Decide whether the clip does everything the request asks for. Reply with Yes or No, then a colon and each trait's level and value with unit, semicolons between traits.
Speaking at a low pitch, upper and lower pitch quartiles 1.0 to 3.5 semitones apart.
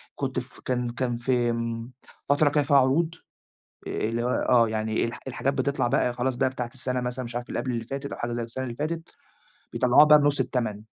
Yes: low, 125 Hz; narrow, 2.5 semitones